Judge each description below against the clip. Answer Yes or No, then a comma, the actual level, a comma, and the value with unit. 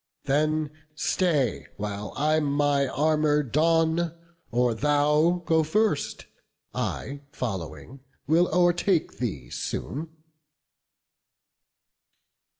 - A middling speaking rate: No, slow, 80 wpm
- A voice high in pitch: No, medium, 150 Hz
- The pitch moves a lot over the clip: No, average, 3.6 semitones